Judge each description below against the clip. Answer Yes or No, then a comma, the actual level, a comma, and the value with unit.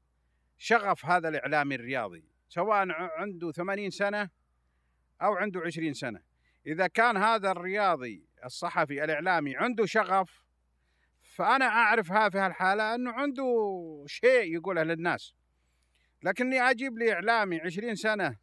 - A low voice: No, medium, 180 Hz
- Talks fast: No, average, 115 wpm